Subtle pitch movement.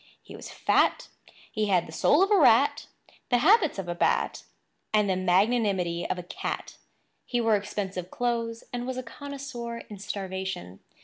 No: average, 4.6 semitones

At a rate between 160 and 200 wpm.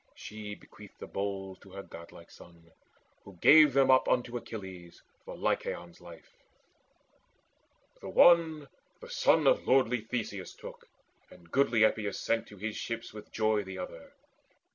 No: average, 145 wpm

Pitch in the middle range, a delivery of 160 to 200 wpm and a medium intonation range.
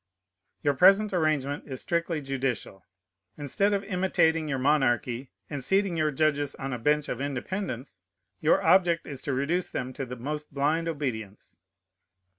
No: medium, 145 Hz; average, 150 wpm; average, 3.9 semitones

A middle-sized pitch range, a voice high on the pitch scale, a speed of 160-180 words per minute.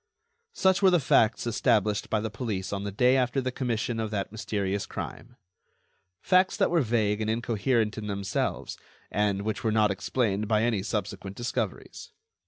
No: average, 3.1 semitones; low, 110 Hz; average, 170 wpm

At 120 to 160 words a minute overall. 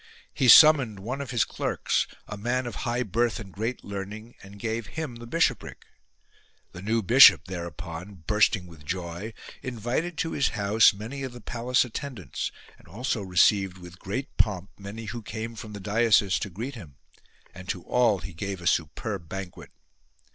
No: average, 170 wpm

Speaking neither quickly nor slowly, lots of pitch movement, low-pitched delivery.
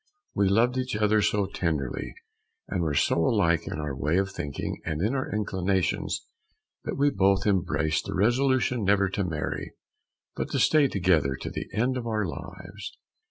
No: average, 165 wpm; average, 4.8 semitones; very low, 95 Hz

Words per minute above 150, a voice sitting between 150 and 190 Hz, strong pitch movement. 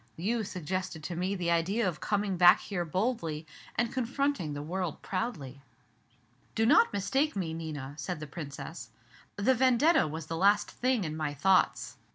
Yes: average, 165 wpm; medium, 185 Hz; wide, 6.1 semitones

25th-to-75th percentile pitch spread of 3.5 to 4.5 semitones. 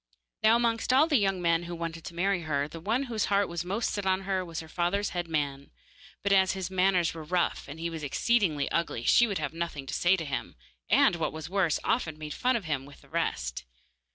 Yes: average, 3.9 semitones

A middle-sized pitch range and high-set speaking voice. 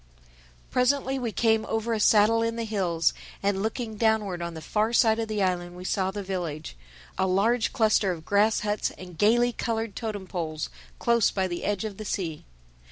Yes: average, 3.5 semitones; high, 210 Hz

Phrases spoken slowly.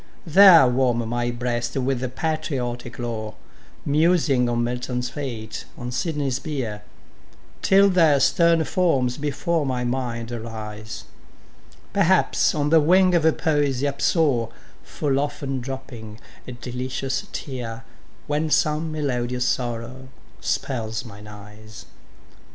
Yes: slow, 110 wpm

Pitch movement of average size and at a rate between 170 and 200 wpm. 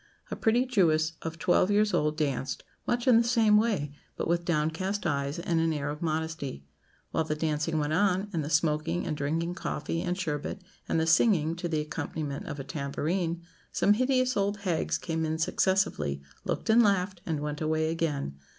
Yes: average, 4.0 semitones; average, 185 wpm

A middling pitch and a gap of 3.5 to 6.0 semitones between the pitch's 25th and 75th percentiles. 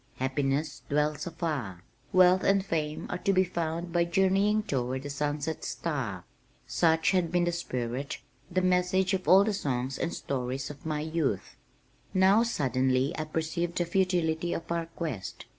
Yes: medium, 160 Hz; average, 4.5 semitones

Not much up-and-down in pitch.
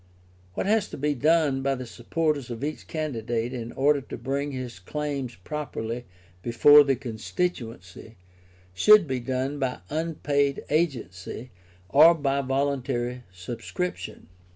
No: average, 3.7 semitones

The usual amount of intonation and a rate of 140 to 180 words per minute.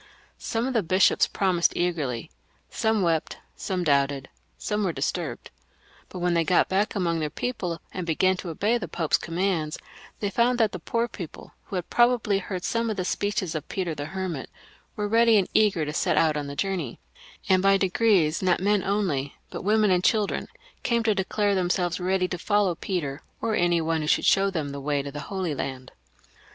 No: average, 4.1 semitones; fast, 205 wpm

